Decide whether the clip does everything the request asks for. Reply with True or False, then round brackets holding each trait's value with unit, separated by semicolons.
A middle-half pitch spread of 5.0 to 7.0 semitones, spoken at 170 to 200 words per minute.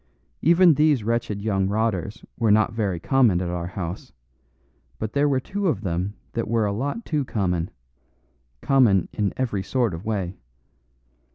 False (5.3 semitones; 160 wpm)